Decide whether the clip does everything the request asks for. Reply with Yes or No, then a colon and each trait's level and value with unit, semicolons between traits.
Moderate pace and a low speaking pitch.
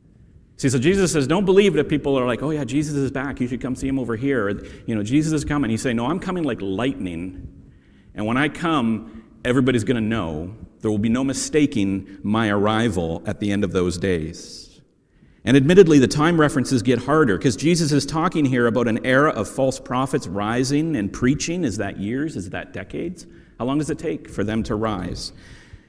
No: fast, 210 wpm; low, 130 Hz